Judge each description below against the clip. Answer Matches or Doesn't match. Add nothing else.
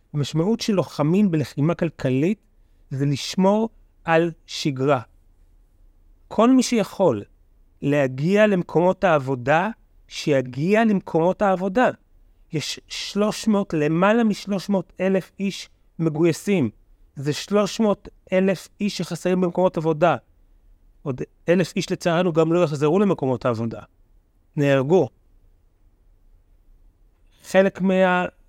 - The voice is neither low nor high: Matches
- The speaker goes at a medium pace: Doesn't match